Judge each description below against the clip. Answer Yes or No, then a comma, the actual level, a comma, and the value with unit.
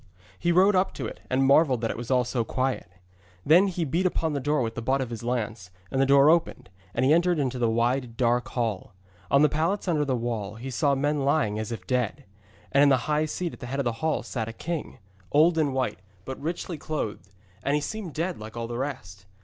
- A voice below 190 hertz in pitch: Yes, low, 135 Hz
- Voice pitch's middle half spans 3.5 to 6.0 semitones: Yes, average, 4.7 semitones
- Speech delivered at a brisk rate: Yes, fast, 240 wpm